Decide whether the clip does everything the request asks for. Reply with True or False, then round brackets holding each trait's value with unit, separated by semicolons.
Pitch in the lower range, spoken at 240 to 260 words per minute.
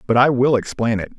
True (125 Hz; 255 wpm)